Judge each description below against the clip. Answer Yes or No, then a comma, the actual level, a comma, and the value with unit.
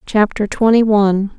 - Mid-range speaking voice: No, high, 210 Hz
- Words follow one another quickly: No, slow, 130 wpm